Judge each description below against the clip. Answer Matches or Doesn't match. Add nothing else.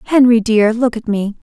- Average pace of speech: Matches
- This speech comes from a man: Doesn't match